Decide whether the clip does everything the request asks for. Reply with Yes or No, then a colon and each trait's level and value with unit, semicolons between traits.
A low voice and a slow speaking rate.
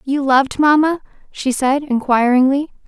No: very high, 275 Hz; slow, 125 wpm